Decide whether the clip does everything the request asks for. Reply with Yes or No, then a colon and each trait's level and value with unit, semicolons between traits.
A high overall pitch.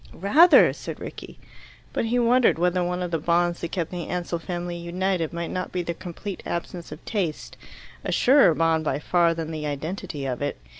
No: medium, 175 Hz